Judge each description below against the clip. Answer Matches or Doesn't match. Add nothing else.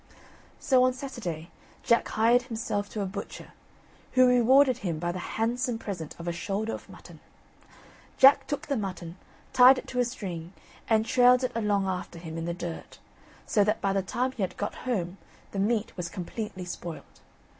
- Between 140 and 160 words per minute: Doesn't match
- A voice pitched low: Doesn't match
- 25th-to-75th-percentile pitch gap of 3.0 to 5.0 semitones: Doesn't match